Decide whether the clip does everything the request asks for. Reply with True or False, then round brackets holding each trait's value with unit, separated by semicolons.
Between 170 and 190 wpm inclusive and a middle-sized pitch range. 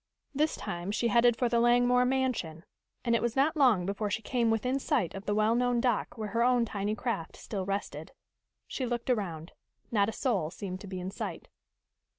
False (200 wpm; 3.7 semitones)